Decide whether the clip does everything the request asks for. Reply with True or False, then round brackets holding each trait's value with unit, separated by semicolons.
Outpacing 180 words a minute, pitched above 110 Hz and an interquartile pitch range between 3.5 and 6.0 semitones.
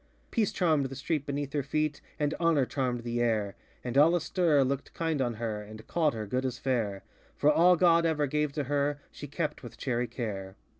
True (205 wpm; 140 Hz; 4.2 semitones)